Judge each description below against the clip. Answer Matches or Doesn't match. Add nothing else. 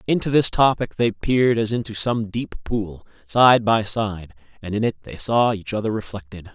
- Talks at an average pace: Matches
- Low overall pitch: Matches